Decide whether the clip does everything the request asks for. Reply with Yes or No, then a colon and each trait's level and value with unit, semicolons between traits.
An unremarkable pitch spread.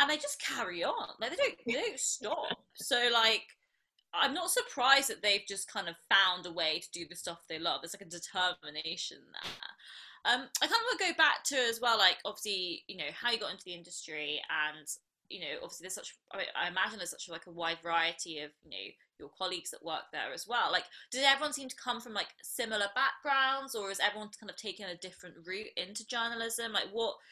No: wide, 6.3 semitones